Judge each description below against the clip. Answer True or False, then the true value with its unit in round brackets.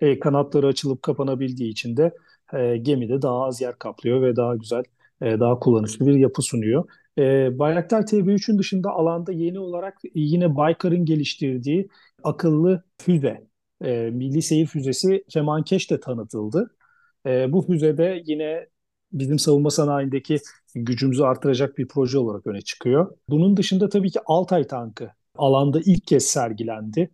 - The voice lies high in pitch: False (145 Hz)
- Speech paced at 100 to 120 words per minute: False (140 wpm)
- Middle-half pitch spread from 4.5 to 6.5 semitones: True (5.1 semitones)